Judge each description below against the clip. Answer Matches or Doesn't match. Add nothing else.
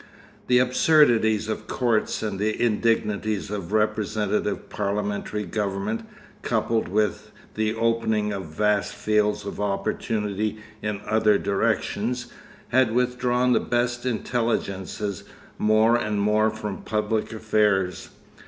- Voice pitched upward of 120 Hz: Doesn't match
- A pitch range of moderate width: Doesn't match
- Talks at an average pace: Doesn't match